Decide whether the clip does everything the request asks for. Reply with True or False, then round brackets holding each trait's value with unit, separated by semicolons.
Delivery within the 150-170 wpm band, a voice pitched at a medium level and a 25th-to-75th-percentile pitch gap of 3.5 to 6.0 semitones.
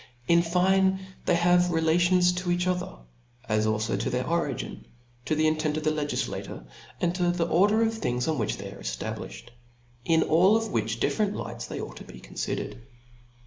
False (185 wpm; 170 Hz; 3.8 semitones)